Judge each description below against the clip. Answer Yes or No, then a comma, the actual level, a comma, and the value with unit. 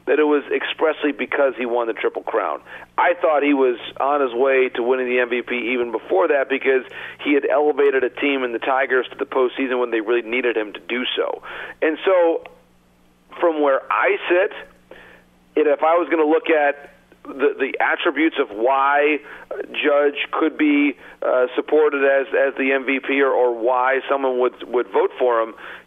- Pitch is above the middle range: No, low, 135 Hz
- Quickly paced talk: No, average, 185 wpm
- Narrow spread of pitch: No, average, 3.9 semitones